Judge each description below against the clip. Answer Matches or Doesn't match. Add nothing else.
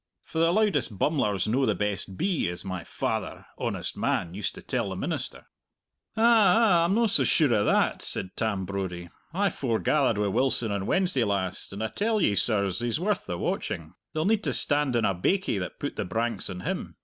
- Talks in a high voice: Doesn't match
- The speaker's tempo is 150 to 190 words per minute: Doesn't match